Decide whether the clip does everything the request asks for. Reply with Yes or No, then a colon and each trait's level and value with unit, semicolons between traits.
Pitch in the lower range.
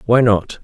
Yes: low, 115 Hz